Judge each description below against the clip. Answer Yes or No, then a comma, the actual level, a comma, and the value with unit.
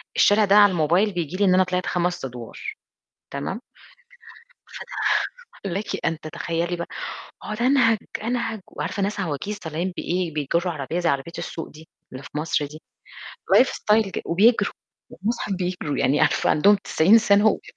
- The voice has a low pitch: No, medium, 180 Hz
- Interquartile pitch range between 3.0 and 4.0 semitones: No, average, 4.6 semitones